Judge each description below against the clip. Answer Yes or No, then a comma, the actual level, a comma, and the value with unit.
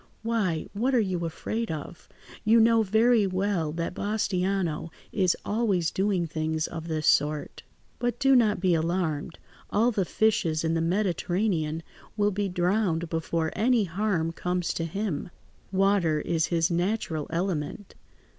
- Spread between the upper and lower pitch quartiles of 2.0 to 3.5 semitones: No, average, 4.2 semitones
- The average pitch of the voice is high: No, medium, 180 Hz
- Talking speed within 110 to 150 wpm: Yes, average, 145 wpm